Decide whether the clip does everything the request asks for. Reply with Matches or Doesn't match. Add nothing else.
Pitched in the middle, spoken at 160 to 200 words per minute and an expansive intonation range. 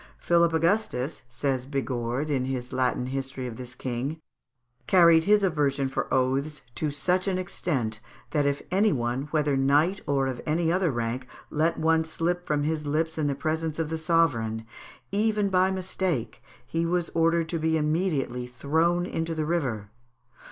Doesn't match